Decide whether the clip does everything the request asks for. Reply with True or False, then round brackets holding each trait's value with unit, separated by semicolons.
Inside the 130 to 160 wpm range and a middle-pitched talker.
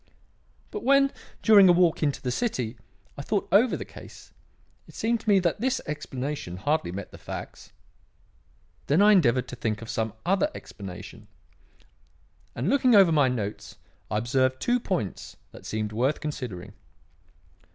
True (155 wpm; 150 Hz)